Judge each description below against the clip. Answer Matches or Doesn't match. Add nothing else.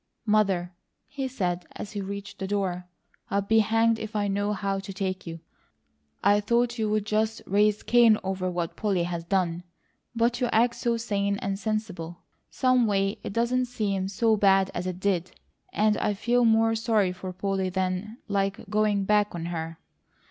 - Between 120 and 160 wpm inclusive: Doesn't match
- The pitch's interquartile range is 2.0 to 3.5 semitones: Matches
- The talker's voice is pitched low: Doesn't match